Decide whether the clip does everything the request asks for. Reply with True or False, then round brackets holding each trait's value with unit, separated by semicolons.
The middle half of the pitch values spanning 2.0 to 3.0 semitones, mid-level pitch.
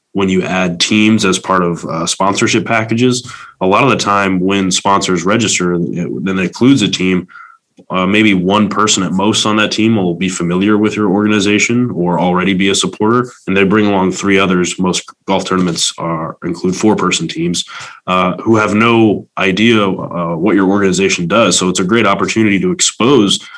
False (2.6 semitones; 100 Hz)